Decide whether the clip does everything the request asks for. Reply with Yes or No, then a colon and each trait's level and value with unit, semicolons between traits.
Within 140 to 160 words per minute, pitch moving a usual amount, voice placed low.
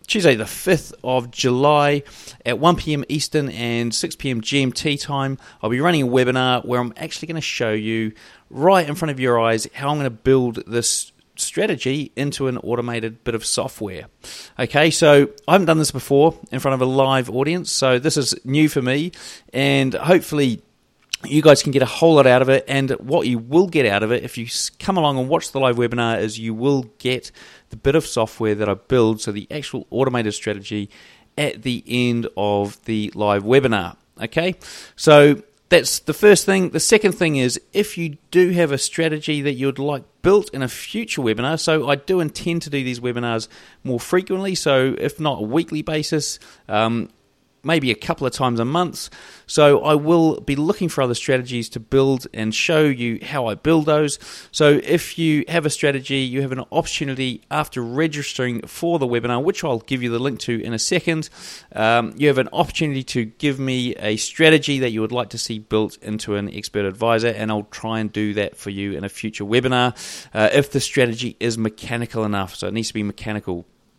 No: fast, 205 wpm; average, 4.7 semitones; low, 130 Hz